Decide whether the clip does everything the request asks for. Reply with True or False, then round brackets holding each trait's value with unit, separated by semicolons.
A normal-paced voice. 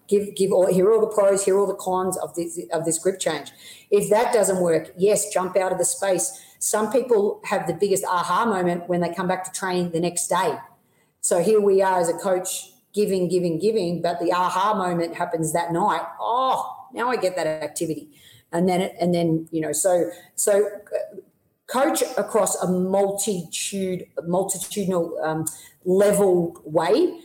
True (180 wpm)